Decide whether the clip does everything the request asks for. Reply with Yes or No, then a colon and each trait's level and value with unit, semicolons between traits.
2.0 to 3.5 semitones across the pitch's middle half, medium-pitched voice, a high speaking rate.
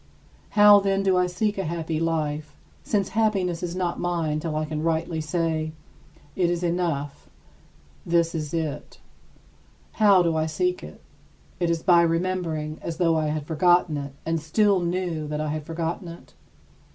No: narrow, 2.5 semitones; medium, 165 Hz; average, 165 wpm